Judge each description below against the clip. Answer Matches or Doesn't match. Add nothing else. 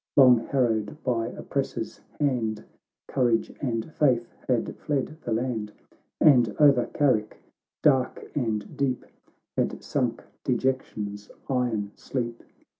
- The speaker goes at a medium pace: Doesn't match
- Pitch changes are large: Doesn't match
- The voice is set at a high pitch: Doesn't match